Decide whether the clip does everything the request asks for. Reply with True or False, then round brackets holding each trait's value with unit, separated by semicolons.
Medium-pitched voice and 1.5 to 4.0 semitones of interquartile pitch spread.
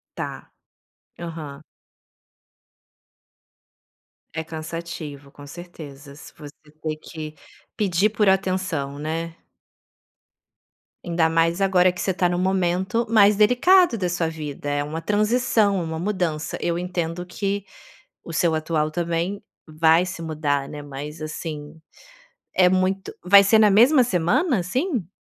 True (170 Hz; 3.7 semitones)